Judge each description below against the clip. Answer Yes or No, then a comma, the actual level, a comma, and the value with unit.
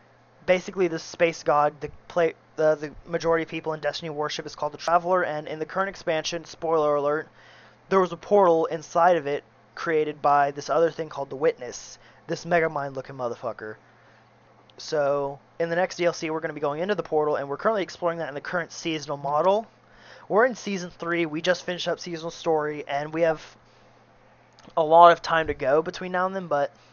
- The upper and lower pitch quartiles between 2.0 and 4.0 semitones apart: Yes, average, 2.9 semitones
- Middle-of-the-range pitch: Yes, medium, 160 Hz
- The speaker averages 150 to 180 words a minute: No, fast, 205 wpm